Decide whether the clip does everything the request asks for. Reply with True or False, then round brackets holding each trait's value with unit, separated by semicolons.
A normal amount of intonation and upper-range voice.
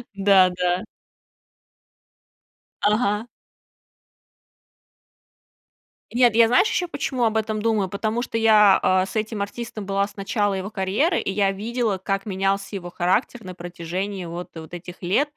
True (3.1 semitones; 200 Hz)